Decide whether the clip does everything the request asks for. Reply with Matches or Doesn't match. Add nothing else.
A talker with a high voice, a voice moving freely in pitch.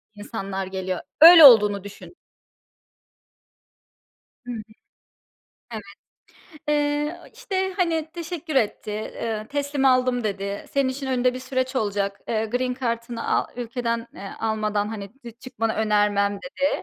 Doesn't match